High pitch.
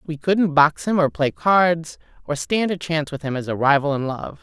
No: medium, 160 Hz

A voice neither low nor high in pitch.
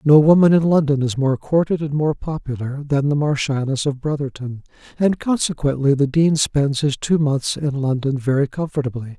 Yes: medium, 145 Hz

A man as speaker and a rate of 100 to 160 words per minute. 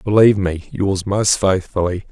Yes: male; average, 140 wpm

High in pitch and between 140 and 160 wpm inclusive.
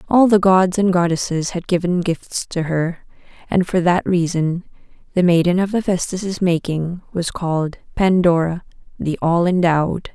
No: medium, 175 Hz; average, 150 wpm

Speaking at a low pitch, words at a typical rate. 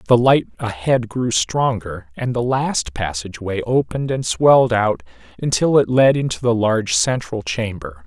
Yes: low, 115 Hz; average, 155 wpm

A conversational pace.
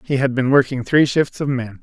No: fast, 265 wpm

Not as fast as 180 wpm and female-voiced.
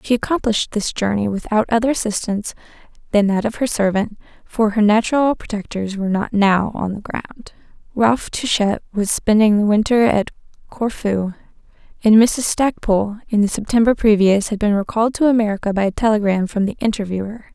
Yes: average, 165 wpm; female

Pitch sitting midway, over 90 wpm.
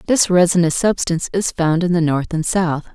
Yes: medium, 175 Hz; fast, 205 wpm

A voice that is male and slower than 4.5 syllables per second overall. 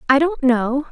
No: female; 4.2 syllables/s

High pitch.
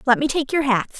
Yes: very high, 265 Hz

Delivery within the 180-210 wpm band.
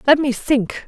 Yes: fast, 205 wpm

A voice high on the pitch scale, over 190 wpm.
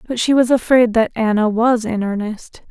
Yes: high, 230 Hz; average, 200 wpm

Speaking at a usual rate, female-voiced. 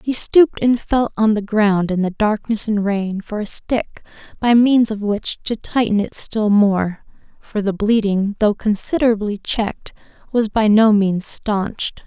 Yes: average, 175 wpm; female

